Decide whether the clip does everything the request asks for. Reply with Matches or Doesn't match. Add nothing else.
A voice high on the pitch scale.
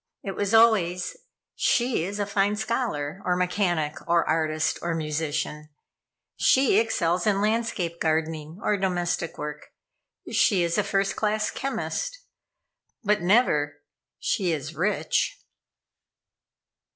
Doesn't match